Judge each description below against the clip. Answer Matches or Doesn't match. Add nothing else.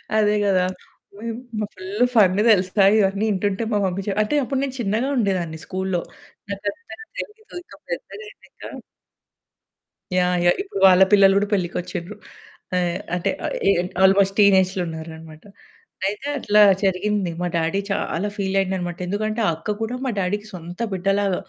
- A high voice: Matches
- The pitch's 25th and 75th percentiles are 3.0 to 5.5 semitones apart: Doesn't match